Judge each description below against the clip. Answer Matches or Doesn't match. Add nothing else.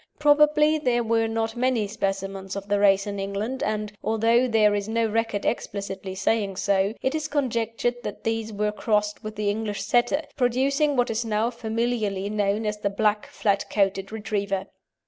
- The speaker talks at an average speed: Matches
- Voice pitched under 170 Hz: Doesn't match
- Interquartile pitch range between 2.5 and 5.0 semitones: Matches